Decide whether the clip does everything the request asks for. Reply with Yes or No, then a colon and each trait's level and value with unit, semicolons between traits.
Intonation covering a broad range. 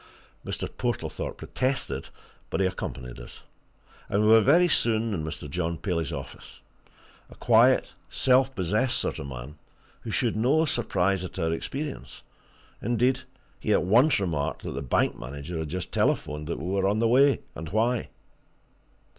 Yes: wide, 7.3 semitones